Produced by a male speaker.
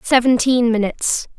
No: female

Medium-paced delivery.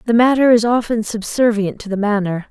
Yes: average, 190 wpm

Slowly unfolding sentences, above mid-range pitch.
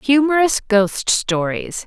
Yes: slow, 95 wpm; high, 240 Hz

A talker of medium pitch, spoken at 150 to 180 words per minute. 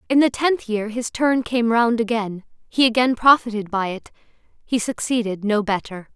No: high, 230 Hz; average, 175 wpm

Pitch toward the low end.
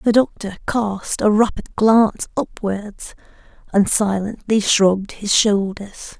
No: high, 210 Hz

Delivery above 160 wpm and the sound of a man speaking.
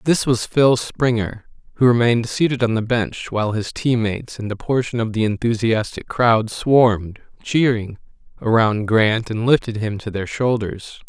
Yes: average, 170 wpm; male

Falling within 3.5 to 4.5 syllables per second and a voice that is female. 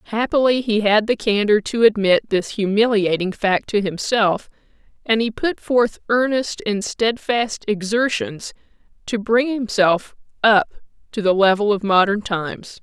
Yes: 4.3 syllables/s; female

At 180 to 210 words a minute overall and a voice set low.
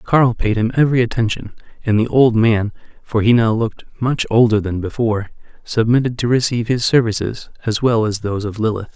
Yes: average, 190 wpm; low, 115 Hz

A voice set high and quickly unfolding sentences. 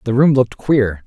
No: low, 120 Hz; fast, 225 wpm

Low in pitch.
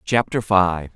Yes: low, 100 Hz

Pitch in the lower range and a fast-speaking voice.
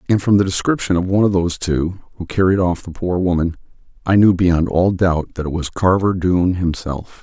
Yes: very low, 90 Hz; fast, 215 wpm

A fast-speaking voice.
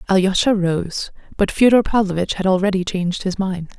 No: average, 160 wpm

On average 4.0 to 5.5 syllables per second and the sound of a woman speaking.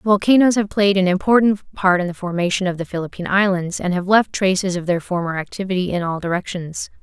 No: 6.0 syllables/s; female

